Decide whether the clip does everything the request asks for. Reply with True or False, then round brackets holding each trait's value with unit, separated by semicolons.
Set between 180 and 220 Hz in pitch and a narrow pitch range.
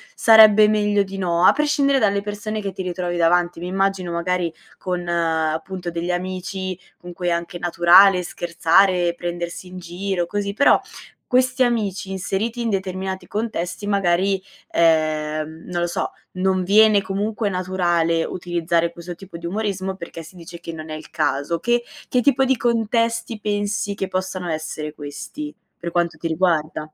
False (185 Hz; 3.1 semitones)